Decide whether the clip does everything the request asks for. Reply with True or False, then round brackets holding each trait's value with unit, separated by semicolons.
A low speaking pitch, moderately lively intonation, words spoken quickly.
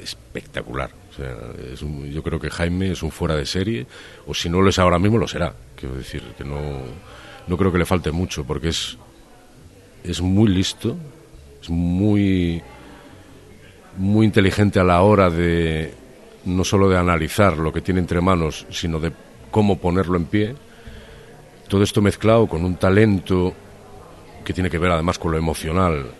False (90 Hz; 3.4 semitones; 170 wpm)